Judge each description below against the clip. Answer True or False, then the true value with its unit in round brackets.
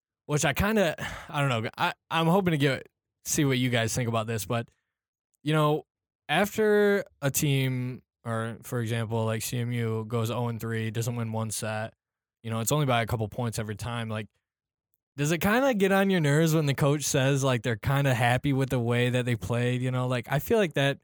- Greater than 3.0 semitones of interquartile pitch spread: True (4.3 semitones)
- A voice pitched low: True (125 Hz)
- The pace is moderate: False (225 wpm)